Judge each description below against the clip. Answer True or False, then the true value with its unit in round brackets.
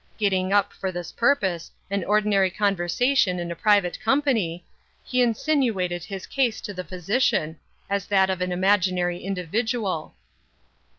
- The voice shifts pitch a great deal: False (3.2 semitones)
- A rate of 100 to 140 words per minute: True (135 wpm)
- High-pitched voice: True (195 Hz)